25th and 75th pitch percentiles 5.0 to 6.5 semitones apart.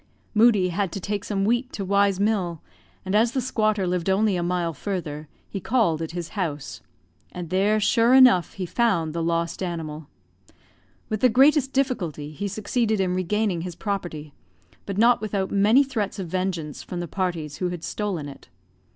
No: average, 4.0 semitones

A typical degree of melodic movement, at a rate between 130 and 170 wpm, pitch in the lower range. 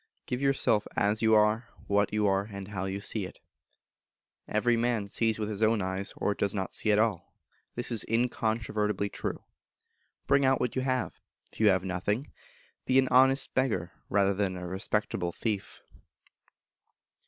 Yes: average, 3.0 semitones; average, 165 wpm; low, 105 Hz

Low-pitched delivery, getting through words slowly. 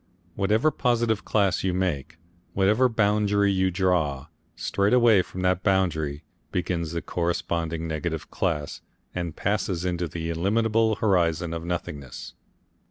Yes: very low, 90 Hz; slow, 125 wpm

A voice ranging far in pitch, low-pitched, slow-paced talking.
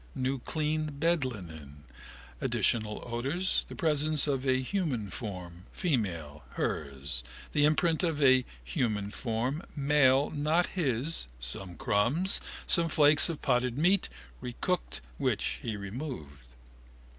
Yes: wide, 7.1 semitones; low, 130 Hz; slow, 115 wpm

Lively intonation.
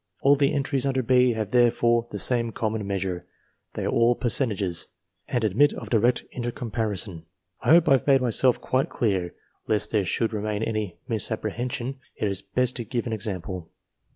No: average, 3.5 semitones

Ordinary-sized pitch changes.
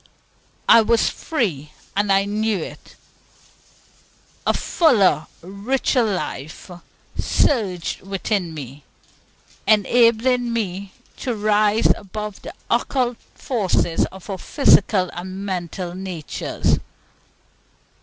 Yes: average, 3.9 semitones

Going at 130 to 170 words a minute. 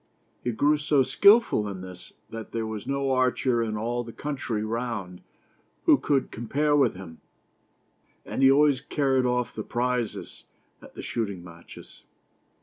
Yes: average, 150 wpm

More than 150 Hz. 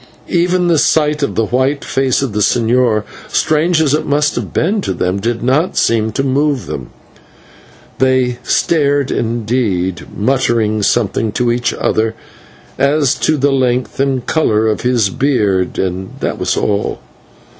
No: low, 125 Hz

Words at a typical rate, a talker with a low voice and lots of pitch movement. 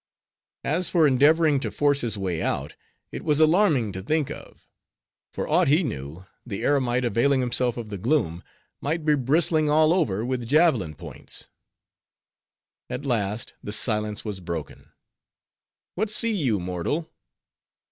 Yes: average, 145 wpm; low, 130 Hz; wide, 6.7 semitones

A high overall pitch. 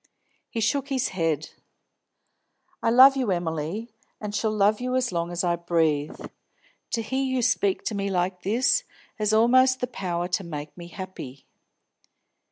Yes: high, 200 Hz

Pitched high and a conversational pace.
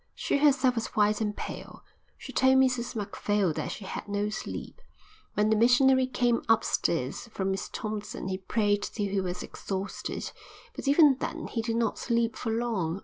Yes: high, 220 Hz; average, 175 wpm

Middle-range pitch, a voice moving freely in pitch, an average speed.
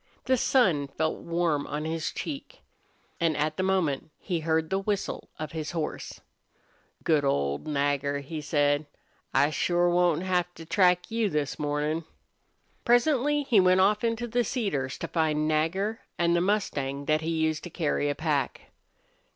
No: medium, 165 Hz; average, 4.2 semitones; average, 160 wpm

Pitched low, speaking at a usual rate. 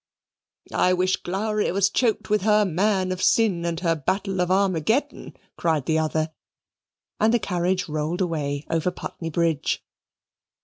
No: medium, 180 Hz; average, 145 wpm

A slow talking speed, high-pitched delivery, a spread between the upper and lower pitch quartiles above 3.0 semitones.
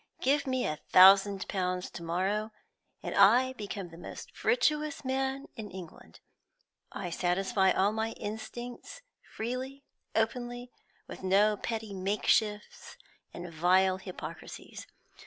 Yes: slow, 120 wpm; high, 210 Hz; average, 4.7 semitones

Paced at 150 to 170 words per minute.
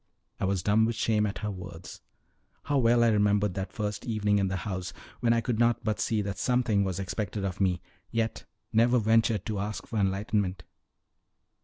No: average, 190 wpm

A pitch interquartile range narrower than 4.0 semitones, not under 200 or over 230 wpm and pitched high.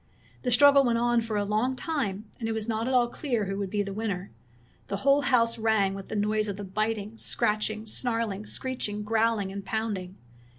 Yes: narrow, 2.5 semitones; fast, 205 wpm; high, 220 Hz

